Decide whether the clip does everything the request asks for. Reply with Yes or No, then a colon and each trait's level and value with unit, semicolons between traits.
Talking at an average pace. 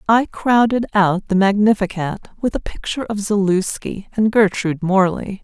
Yes: average, 145 wpm